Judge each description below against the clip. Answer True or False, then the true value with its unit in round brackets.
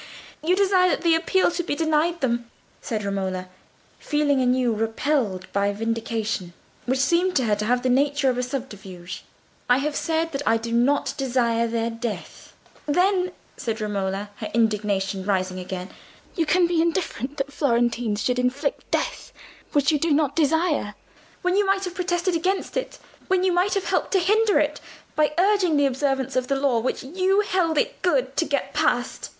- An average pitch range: False (6.9 semitones)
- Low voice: False (275 Hz)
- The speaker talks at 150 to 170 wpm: False (180 wpm)